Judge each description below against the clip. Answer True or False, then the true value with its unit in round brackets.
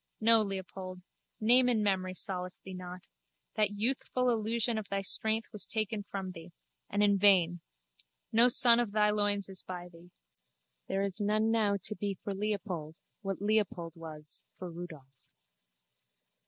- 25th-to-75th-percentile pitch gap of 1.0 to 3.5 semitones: True (2.8 semitones)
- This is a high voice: True (200 Hz)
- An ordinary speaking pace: True (150 wpm)